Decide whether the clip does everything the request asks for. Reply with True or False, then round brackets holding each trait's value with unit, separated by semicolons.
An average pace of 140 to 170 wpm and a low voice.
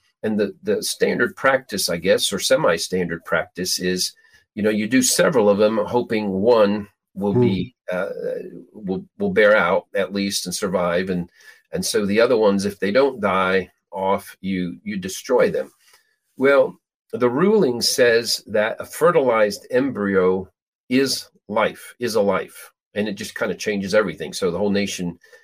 True (165 wpm; 105 Hz)